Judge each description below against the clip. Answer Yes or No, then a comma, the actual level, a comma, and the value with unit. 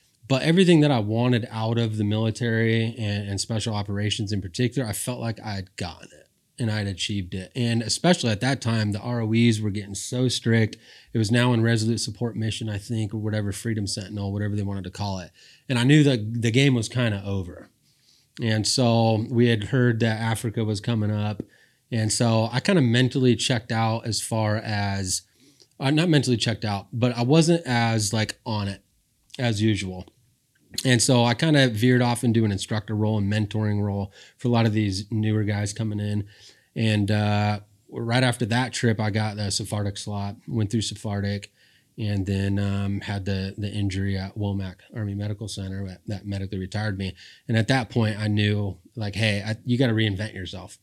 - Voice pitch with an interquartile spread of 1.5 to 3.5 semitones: Yes, narrow, 2.6 semitones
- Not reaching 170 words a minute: No, average, 200 wpm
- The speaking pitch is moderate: No, low, 110 Hz